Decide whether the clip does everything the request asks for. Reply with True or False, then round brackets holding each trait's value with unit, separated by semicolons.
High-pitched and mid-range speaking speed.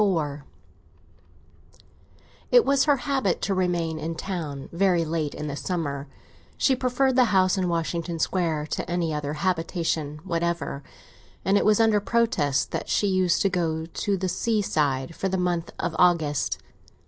False (175 Hz; 155 wpm)